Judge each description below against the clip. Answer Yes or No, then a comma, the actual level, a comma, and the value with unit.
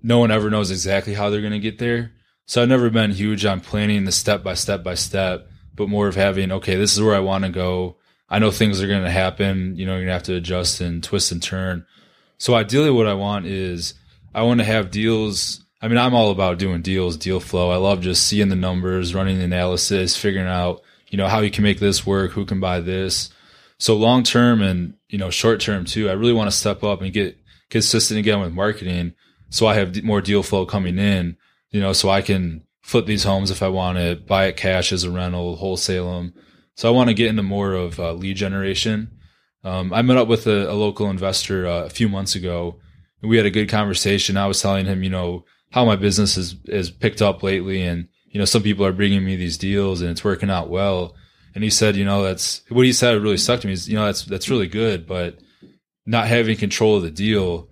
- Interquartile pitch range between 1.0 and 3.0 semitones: Yes, narrow, 2.6 semitones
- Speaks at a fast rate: Yes, fast, 245 wpm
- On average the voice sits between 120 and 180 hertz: No, low, 100 Hz